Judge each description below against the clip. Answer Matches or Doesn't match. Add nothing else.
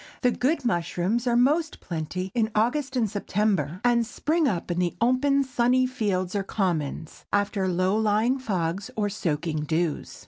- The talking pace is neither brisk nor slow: Matches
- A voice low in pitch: Doesn't match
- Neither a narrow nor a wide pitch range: Doesn't match